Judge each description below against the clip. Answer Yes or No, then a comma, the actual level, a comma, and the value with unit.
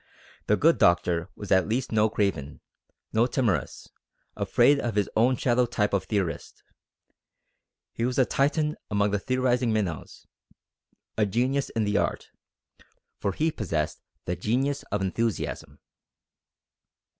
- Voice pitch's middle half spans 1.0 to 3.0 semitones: No, average, 4.5 semitones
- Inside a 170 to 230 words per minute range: No, slow, 135 wpm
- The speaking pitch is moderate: No, low, 110 Hz